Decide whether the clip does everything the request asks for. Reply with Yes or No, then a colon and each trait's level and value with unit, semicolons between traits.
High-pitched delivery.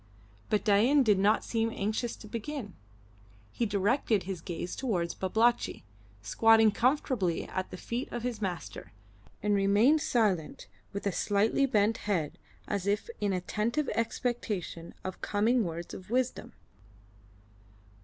Yes: high, 210 Hz